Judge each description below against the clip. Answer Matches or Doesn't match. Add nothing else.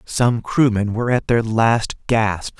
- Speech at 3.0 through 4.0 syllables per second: Matches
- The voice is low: Matches